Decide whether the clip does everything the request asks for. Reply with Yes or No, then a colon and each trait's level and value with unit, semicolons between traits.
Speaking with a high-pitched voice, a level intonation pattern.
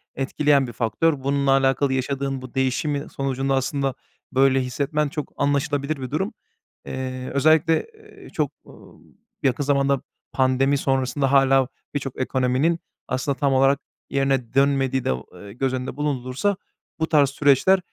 No: low, 135 Hz; narrow, 1.5 semitones